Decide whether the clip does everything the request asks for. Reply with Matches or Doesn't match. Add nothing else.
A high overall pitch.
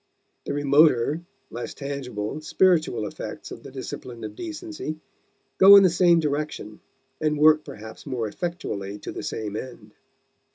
Doesn't match